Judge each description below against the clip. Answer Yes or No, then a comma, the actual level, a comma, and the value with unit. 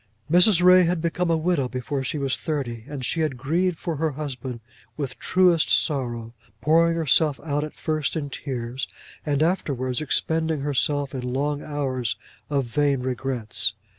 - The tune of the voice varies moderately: Yes, average, 3.7 semitones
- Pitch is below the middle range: No, medium, 145 Hz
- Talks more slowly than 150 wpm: No, average, 160 wpm